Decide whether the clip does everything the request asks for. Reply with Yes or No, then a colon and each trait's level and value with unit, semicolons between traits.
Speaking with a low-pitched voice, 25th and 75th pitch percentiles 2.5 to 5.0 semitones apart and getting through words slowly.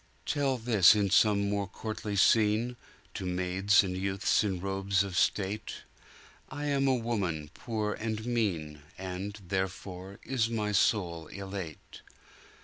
Yes: low, 100 Hz; average, 2.8 semitones; slow, 120 wpm